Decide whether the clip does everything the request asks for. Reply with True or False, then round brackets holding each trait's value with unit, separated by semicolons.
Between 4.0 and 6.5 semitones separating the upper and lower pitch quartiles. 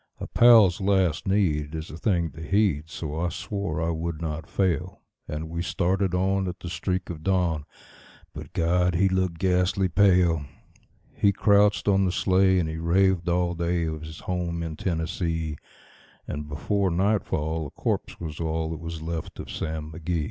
False (2.8 semitones)